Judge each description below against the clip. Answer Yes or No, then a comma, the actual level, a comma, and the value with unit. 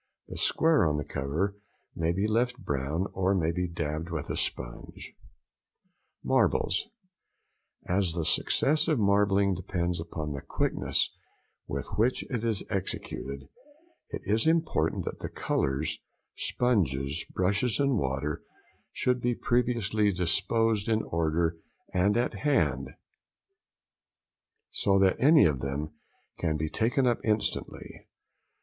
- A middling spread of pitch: No, wide, 6.5 semitones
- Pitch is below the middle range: Yes, very low, 95 Hz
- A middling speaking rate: No, slow, 125 wpm